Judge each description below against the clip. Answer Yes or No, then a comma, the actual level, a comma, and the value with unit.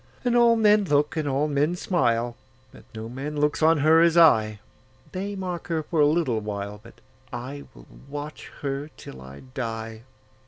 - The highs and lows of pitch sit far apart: Yes, wide, 5.9 semitones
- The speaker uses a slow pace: No, average, 160 wpm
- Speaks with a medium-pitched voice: Yes, medium, 145 Hz